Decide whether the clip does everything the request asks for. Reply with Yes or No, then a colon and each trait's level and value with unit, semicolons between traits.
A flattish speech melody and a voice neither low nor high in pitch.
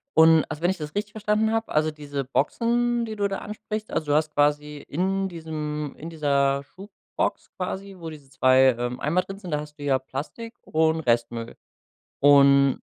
No: wide, 5.5 semitones; medium, 155 Hz